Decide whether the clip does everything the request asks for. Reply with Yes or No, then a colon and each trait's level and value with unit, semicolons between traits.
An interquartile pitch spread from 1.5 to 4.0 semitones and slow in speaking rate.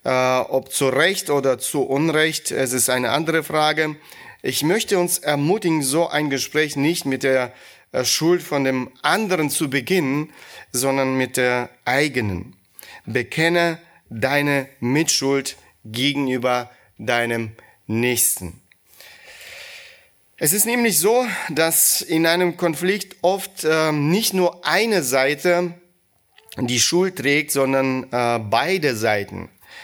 No: average, 4.9 semitones; slow, 115 wpm